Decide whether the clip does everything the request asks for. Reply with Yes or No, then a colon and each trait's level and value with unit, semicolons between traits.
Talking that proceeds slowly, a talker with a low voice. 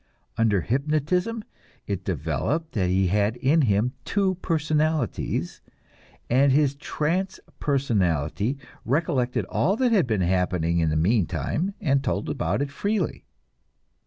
Yes: slow, 125 wpm; low, 130 Hz